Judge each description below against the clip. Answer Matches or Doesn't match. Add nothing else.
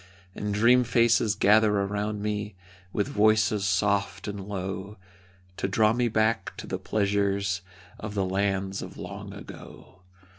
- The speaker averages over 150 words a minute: Doesn't match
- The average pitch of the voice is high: Doesn't match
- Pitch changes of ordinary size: Doesn't match